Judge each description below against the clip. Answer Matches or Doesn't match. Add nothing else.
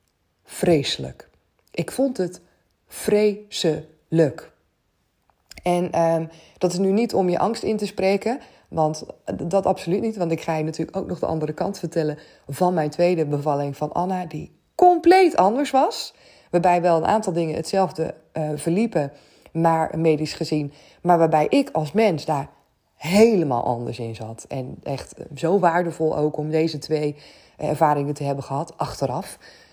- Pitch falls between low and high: Matches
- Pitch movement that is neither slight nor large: Matches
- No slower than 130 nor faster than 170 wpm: Matches